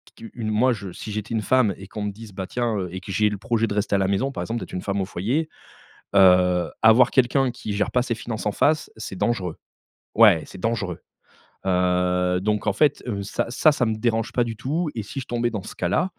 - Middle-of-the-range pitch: No, low, 110 Hz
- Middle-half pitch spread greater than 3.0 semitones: Yes, average, 3.6 semitones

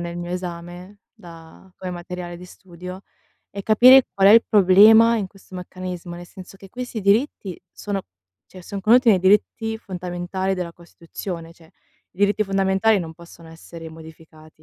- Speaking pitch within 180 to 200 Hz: Yes, medium, 185 Hz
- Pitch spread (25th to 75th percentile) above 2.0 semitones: Yes, average, 2.7 semitones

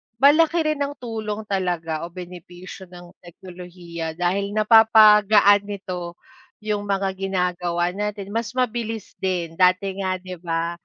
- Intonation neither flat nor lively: Yes, average, 3.2 semitones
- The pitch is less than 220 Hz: Yes, high, 190 Hz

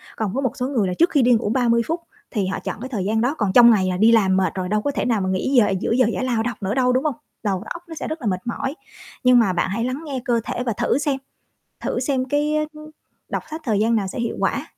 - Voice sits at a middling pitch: No, high, 235 Hz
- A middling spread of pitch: Yes, average, 4.3 semitones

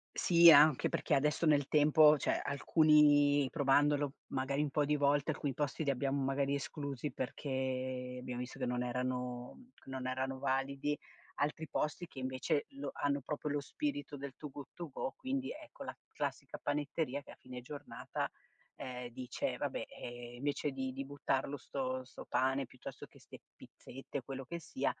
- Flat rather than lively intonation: Yes, narrow, 2.2 semitones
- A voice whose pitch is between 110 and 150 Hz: Yes, medium, 140 Hz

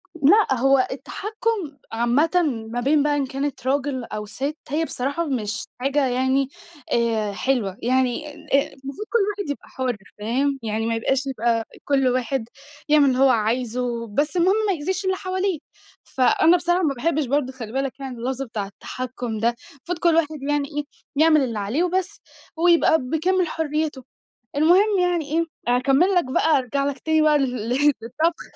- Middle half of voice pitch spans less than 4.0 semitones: No, average, 4.3 semitones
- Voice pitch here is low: No, very high, 275 Hz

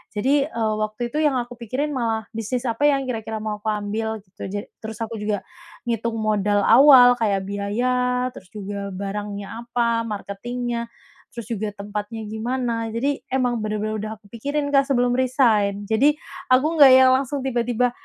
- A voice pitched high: Yes, high, 230 Hz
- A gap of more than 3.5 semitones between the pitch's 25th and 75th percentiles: No, average, 3.2 semitones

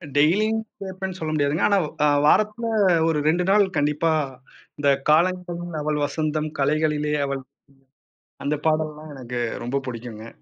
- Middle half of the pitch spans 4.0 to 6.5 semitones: No, average, 3.3 semitones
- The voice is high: No, medium, 155 Hz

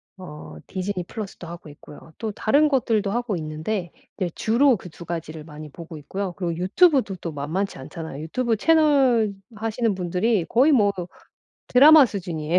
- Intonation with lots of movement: Yes, wide, 5.8 semitones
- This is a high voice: Yes, high, 195 Hz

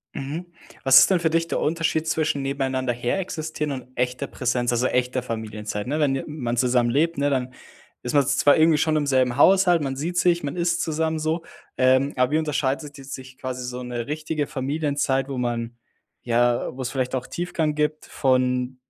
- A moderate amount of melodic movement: Yes, average, 3.7 semitones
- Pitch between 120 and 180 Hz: Yes, low, 135 Hz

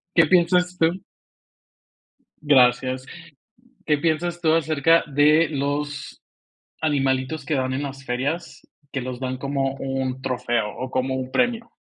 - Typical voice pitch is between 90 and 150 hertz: Yes, medium, 140 Hz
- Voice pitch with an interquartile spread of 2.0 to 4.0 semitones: Yes, average, 3.6 semitones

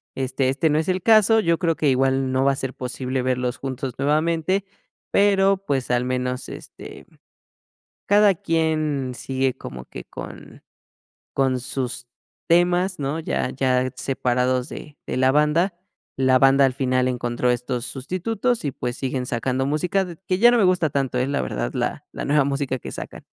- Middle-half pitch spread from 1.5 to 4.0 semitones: No, average, 4.5 semitones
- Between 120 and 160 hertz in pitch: Yes, low, 135 Hz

